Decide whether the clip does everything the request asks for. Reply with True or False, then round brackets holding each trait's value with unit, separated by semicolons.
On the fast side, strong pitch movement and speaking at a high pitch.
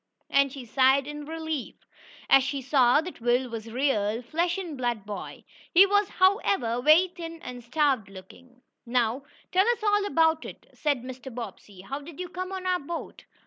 False (185 wpm; 5.7 semitones; 275 Hz)